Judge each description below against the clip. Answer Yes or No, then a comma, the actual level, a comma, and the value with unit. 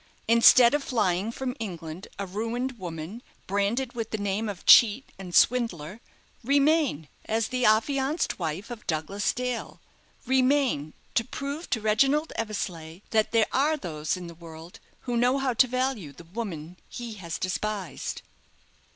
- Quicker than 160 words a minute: No, average, 150 wpm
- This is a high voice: Yes, high, 220 Hz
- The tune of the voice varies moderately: No, wide, 5.9 semitones